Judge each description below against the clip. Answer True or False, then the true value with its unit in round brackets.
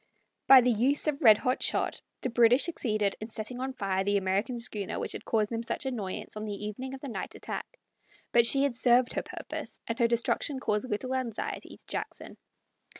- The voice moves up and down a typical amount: True (3.5 semitones)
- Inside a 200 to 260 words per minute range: True (205 wpm)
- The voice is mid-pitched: False (235 Hz)